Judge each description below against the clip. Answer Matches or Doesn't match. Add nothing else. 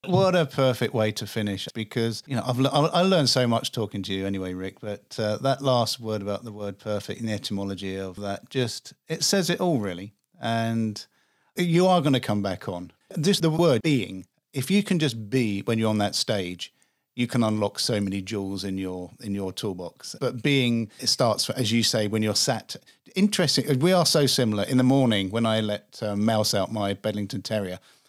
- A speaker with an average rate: Doesn't match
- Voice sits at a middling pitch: Doesn't match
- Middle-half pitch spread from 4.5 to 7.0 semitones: Matches